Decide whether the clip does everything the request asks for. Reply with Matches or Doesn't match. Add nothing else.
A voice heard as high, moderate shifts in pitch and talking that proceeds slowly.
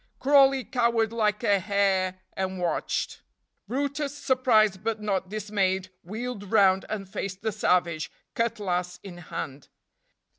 Matches